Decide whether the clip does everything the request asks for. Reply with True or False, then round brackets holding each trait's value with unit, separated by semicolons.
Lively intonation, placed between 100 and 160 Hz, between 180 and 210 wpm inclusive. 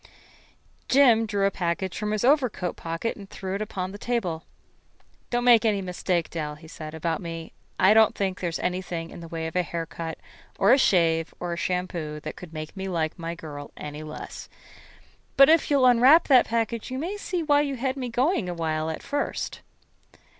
False (6.3 semitones; 185 Hz; 200 wpm)